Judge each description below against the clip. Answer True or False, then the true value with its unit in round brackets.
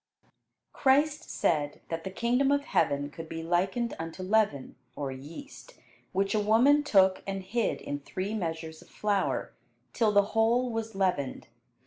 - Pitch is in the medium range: False (195 Hz)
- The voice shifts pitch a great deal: True (6.2 semitones)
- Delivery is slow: False (150 wpm)